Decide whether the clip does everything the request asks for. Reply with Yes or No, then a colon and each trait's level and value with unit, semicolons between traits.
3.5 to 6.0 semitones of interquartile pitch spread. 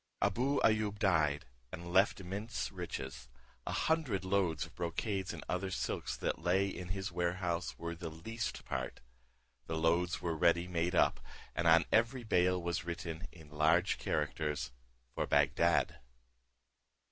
No: average, 3.0 semitones